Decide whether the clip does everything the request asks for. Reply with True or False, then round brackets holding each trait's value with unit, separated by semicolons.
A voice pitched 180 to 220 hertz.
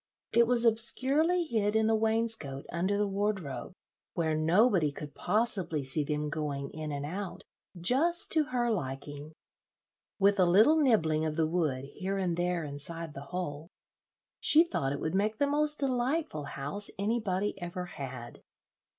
True (185 Hz)